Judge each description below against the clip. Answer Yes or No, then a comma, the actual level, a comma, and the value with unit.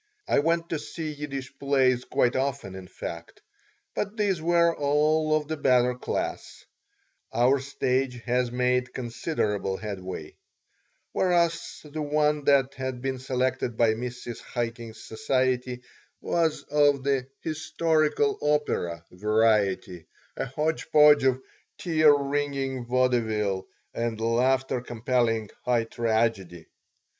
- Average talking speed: No, slow, 115 wpm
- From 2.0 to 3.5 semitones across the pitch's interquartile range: No, average, 4.1 semitones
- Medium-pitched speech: No, low, 130 Hz